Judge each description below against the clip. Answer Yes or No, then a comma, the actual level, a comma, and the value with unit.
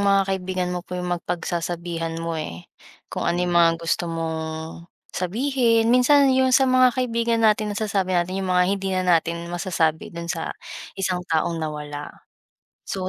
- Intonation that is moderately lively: Yes, average, 4.1 semitones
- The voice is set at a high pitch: No, medium, 180 Hz